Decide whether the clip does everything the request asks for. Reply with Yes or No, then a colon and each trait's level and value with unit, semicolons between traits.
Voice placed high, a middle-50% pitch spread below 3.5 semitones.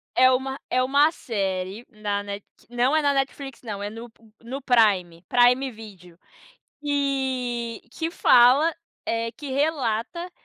No: high, 245 Hz; average, 4.2 semitones